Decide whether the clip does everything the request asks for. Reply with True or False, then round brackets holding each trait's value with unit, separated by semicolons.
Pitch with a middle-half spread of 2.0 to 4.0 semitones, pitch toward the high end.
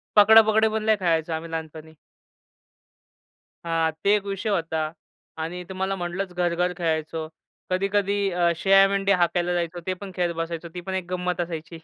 False (2.8 semitones; 180 Hz)